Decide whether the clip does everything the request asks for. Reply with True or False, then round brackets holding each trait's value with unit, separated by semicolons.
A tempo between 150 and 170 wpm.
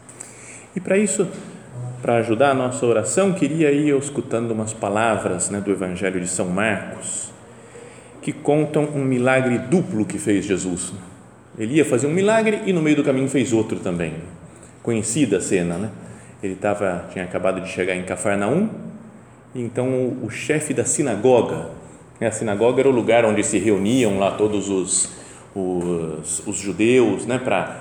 True (165 wpm)